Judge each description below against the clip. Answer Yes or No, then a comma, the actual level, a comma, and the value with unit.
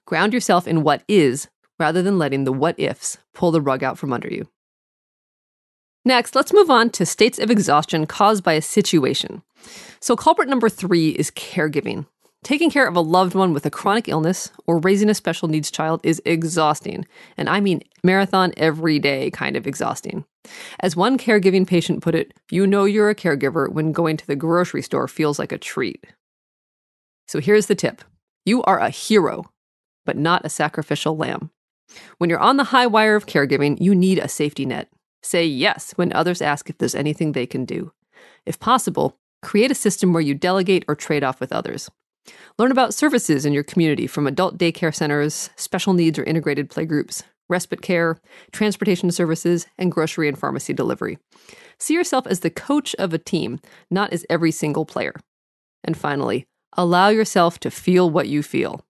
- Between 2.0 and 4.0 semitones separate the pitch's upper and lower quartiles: No, average, 4.4 semitones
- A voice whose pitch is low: No, medium, 175 Hz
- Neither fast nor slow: Yes, average, 185 wpm